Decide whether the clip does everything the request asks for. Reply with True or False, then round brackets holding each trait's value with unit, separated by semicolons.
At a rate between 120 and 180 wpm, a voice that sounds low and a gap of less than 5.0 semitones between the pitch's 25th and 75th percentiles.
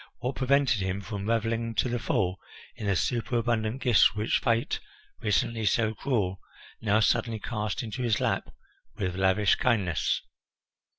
True (140 wpm; 110 Hz; 2.8 semitones)